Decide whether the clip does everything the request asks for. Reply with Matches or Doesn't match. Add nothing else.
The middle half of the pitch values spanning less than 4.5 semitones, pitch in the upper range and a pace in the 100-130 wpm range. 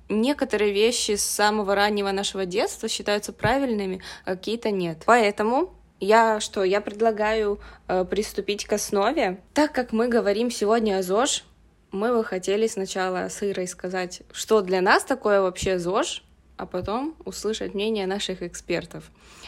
Doesn't match